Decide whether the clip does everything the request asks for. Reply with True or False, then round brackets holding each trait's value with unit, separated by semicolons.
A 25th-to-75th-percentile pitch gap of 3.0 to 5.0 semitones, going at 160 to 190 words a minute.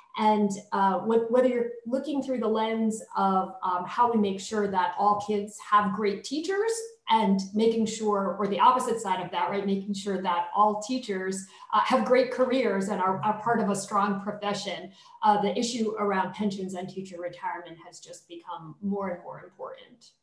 True (3.5 semitones; 185 wpm)